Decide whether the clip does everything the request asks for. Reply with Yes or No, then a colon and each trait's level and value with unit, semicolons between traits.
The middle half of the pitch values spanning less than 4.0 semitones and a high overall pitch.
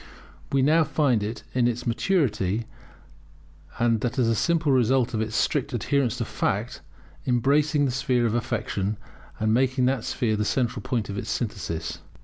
No: average, 3.4 semitones; low, 120 Hz